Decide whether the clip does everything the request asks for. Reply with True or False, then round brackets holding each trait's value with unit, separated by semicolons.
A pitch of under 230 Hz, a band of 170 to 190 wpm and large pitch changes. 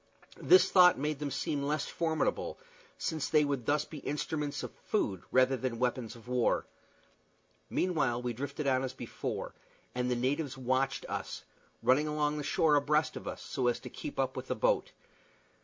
False (140 Hz; 175 wpm; 3.0 semitones)